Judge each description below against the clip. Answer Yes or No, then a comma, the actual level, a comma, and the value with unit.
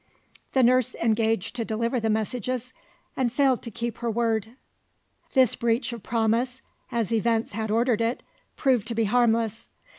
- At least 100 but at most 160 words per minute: Yes, average, 155 wpm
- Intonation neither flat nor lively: No, narrow, 1.7 semitones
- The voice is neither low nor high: No, high, 230 Hz